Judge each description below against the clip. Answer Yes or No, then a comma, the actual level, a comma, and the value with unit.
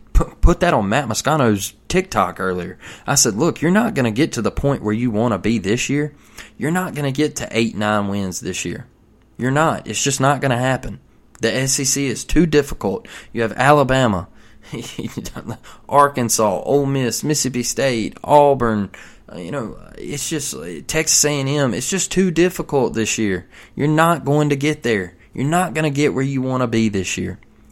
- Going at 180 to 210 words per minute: Yes, average, 190 wpm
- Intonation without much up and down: No, average, 5.1 semitones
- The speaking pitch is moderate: No, low, 130 Hz